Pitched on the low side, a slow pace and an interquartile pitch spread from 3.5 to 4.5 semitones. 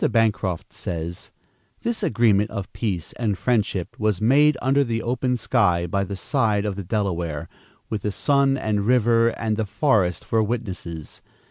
No: low, 105 Hz; average, 155 wpm; average, 3.8 semitones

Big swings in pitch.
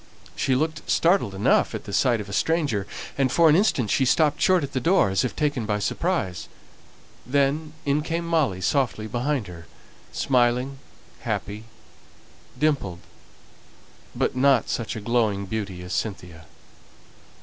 Yes: wide, 6.5 semitones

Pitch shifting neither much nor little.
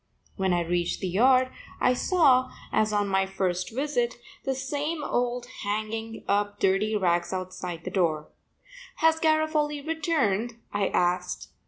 No: wide, 6.2 semitones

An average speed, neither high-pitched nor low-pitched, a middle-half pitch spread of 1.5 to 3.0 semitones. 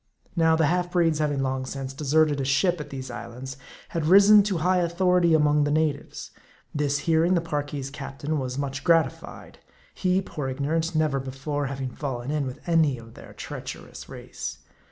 No: average, 175 wpm; medium, 150 Hz; average, 3.5 semitones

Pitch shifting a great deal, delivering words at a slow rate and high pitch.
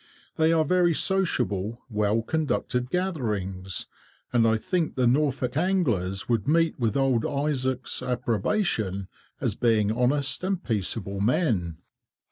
No: wide, 6.8 semitones; slow, 120 wpm; low, 125 Hz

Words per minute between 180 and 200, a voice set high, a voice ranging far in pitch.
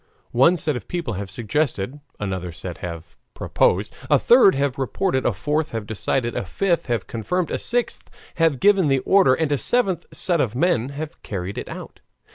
No: average, 185 wpm; low, 135 Hz; wide, 8.0 semitones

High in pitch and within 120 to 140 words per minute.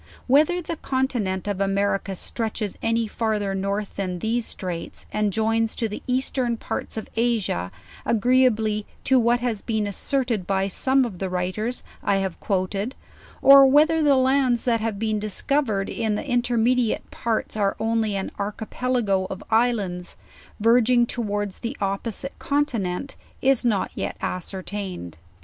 No: high, 220 Hz; average, 150 wpm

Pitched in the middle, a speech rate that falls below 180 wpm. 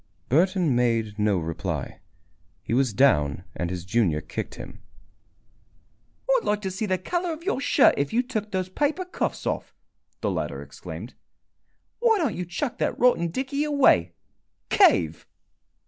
Yes: medium, 180 Hz; average, 150 wpm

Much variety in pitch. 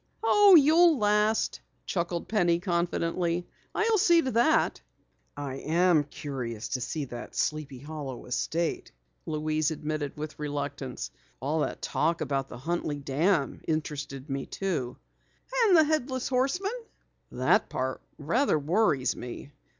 Yes: wide, 7.0 semitones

